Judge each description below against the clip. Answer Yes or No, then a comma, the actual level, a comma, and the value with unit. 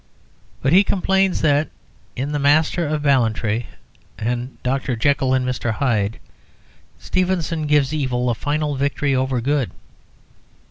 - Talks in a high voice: No, medium, 140 Hz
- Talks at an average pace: No, slow, 130 wpm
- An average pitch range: Yes, average, 3.3 semitones